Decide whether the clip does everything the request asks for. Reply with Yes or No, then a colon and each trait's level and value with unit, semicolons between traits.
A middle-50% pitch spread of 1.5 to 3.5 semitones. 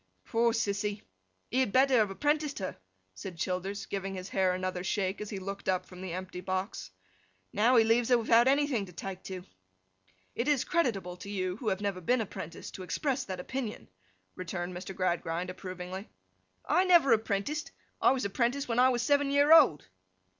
No: average, 5.3 semitones